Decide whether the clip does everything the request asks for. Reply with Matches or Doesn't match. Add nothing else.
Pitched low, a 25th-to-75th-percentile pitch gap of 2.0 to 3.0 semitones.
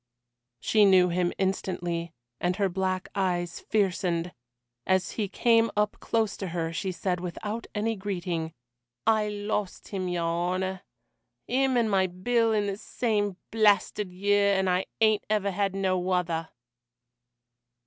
Doesn't match